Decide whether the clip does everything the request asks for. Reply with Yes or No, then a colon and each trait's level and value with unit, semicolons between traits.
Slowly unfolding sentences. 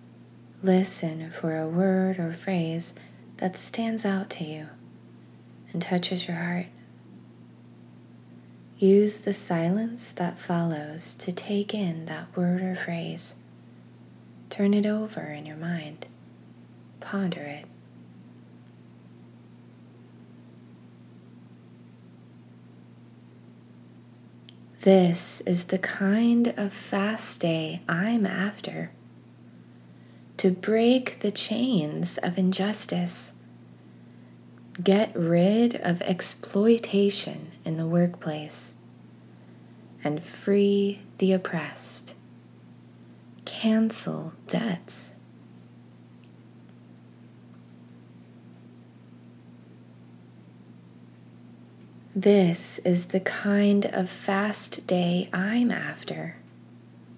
Yes: slow, 75 wpm